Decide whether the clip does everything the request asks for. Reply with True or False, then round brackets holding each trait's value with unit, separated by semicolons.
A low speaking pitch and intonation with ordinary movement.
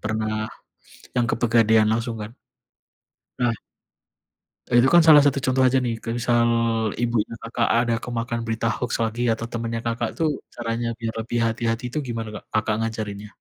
False (115 Hz; 1.2 semitones)